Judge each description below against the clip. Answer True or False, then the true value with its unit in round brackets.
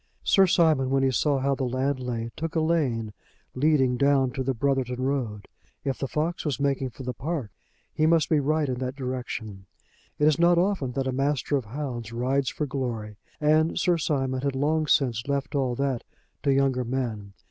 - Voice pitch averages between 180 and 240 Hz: False (135 Hz)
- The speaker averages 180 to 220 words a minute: True (195 wpm)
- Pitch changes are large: False (2.9 semitones)